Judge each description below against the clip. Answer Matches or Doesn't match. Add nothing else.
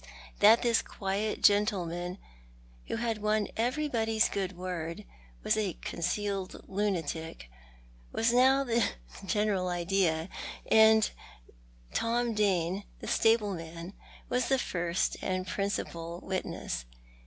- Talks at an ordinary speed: Doesn't match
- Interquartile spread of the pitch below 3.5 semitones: Doesn't match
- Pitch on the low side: Doesn't match